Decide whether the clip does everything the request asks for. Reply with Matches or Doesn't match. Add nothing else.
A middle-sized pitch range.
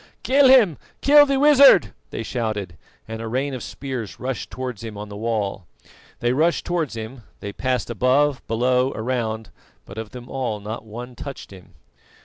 Matches